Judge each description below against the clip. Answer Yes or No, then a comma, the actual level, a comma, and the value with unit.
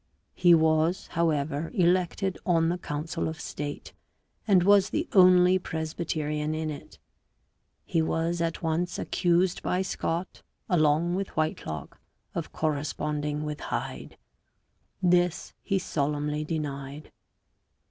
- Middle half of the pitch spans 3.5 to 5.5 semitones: No, average, 2.8 semitones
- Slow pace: Yes, slow, 115 wpm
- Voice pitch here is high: No, medium, 165 Hz